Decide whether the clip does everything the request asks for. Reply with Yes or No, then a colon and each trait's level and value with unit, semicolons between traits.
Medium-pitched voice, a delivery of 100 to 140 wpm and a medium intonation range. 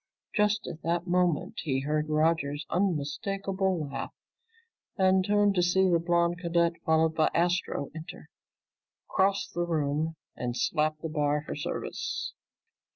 Yes: medium, 170 Hz; slow, 135 wpm; average, 3.3 semitones